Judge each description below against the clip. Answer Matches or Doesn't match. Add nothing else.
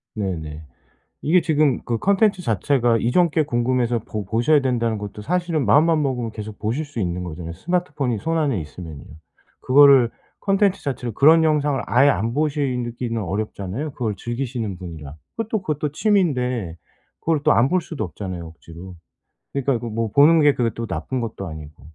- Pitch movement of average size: Doesn't match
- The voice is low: Matches